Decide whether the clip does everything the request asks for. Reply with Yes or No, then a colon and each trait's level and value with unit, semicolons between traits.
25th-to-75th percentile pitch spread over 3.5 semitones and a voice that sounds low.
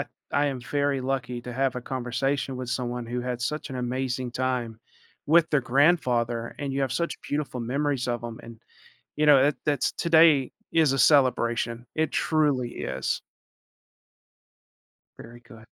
No: average, 2.9 semitones; low, 130 Hz